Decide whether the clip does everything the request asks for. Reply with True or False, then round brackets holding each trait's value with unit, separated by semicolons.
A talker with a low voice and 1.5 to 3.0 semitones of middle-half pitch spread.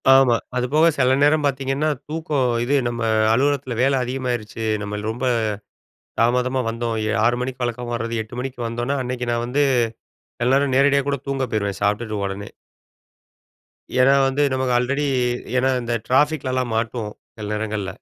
True (125 Hz; 2.6 semitones)